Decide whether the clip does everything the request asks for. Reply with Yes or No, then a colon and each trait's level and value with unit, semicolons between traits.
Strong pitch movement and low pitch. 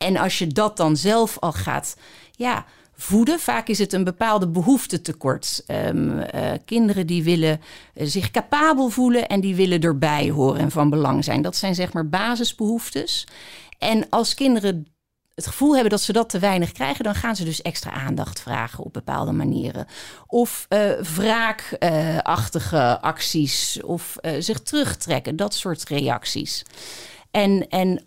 No: wide, 5.8 semitones; high, 190 Hz